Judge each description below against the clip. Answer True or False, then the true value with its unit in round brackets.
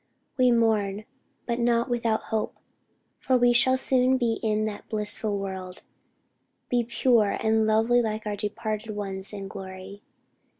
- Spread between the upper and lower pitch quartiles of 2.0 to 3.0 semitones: True (2.5 semitones)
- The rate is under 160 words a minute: True (140 wpm)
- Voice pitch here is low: False (220 Hz)